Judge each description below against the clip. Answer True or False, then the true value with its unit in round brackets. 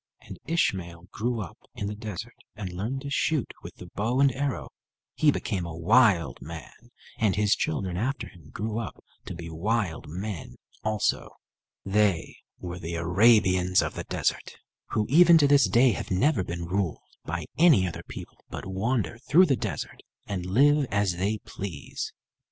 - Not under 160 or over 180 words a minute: True (170 wpm)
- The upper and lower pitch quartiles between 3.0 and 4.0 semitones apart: False (5.4 semitones)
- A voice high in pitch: False (100 Hz)